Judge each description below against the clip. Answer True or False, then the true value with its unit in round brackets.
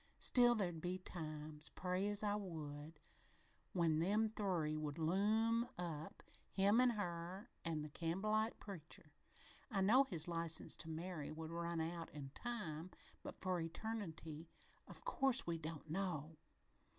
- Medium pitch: True (170 Hz)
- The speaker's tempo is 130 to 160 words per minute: True (140 wpm)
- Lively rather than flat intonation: False (4.4 semitones)